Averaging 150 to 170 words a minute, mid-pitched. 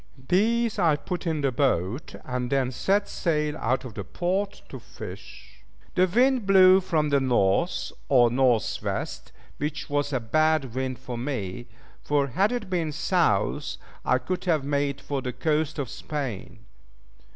Yes: average, 160 wpm; medium, 145 Hz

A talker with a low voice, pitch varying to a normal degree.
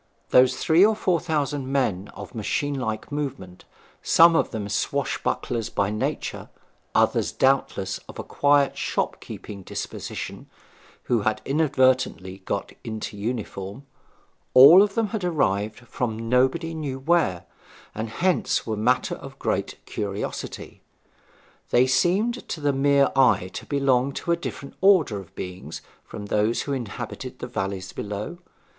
No: low, 130 Hz; wide, 6.0 semitones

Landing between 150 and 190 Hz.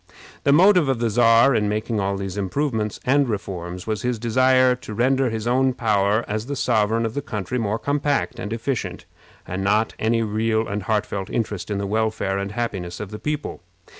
No: low, 110 Hz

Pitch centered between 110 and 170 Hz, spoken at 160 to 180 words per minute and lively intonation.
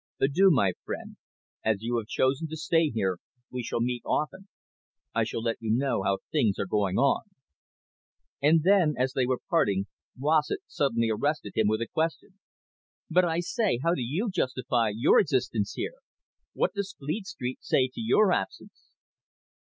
Yes: low, 135 Hz; average, 170 wpm; wide, 6.4 semitones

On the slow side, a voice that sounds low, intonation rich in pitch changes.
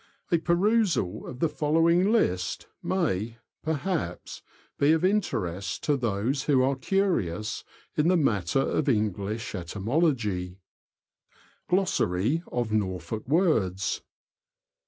Yes: slow, 110 wpm; low, 130 Hz; wide, 9.0 semitones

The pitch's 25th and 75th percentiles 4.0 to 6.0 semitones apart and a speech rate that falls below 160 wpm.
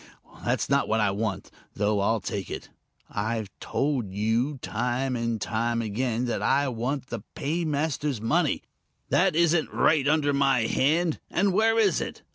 Yes: average, 5.2 semitones; average, 150 wpm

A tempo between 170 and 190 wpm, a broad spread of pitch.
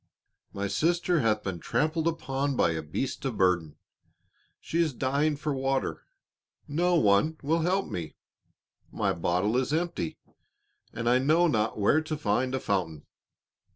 No: average, 150 wpm; wide, 7.8 semitones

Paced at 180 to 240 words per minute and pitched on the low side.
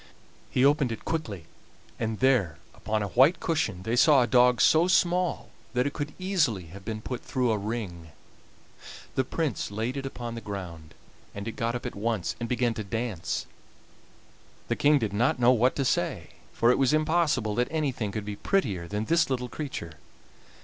Yes: average, 185 wpm; low, 120 Hz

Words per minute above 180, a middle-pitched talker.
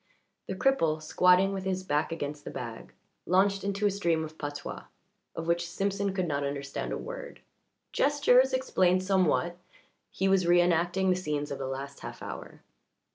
No: average, 165 wpm; medium, 180 Hz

